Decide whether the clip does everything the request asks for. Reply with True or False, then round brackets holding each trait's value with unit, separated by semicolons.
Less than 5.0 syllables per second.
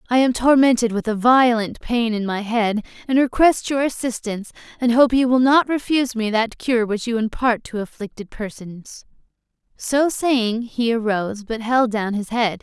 True (4.8 syllables/s)